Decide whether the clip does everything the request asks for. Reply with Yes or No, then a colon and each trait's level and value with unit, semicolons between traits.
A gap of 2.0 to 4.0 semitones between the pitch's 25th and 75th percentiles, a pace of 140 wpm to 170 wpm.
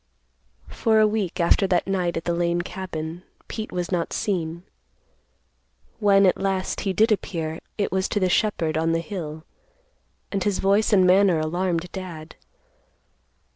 Yes: average, 2.8 semitones; average, 155 wpm